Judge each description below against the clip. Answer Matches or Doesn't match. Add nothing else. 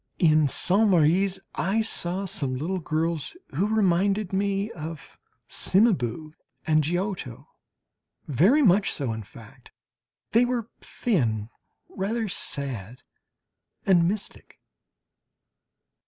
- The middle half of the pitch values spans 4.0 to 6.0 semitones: Matches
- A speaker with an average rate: Doesn't match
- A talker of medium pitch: Matches